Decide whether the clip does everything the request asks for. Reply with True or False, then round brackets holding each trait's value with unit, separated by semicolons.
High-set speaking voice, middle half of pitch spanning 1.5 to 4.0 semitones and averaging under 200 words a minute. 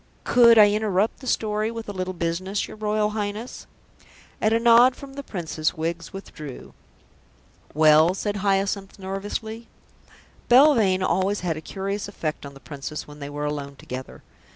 False (195 Hz; 4.9 semitones; 155 wpm)